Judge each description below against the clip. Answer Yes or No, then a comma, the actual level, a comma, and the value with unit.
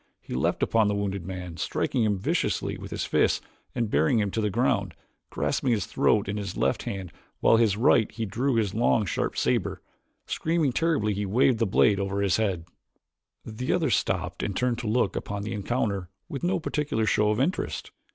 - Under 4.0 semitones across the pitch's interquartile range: Yes, average, 3.4 semitones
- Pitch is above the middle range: No, low, 105 Hz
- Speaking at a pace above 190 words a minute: Yes, average, 200 wpm